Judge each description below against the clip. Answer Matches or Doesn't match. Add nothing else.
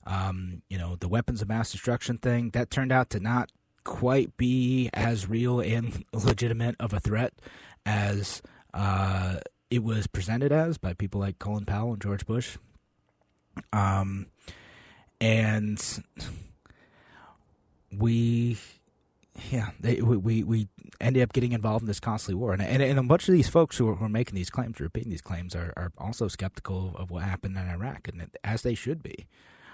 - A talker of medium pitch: Doesn't match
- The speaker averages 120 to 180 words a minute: Matches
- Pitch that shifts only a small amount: Doesn't match